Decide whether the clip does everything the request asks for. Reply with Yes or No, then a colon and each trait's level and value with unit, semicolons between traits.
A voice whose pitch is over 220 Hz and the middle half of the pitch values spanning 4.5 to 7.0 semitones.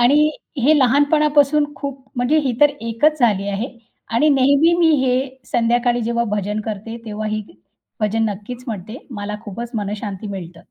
Yes: high, 235 Hz; average, 4.9 semitones